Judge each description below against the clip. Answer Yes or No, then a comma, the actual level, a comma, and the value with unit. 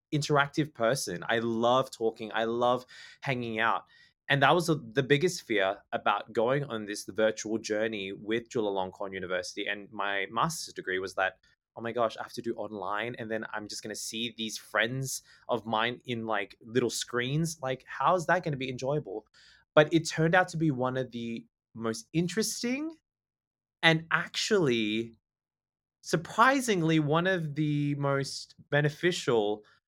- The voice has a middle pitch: No, low, 120 Hz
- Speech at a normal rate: Yes, average, 165 wpm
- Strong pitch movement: Yes, wide, 5.7 semitones